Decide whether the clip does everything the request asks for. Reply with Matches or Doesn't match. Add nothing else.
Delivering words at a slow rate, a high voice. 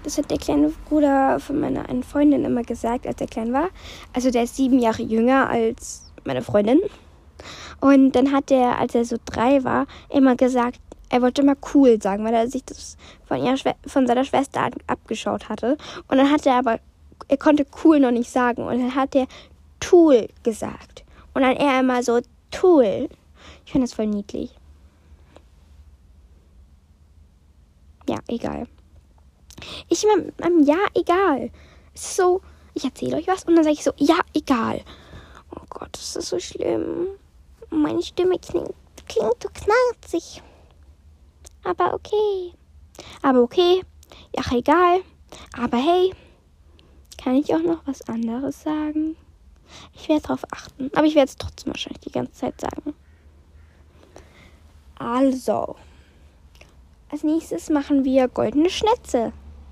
Doesn't match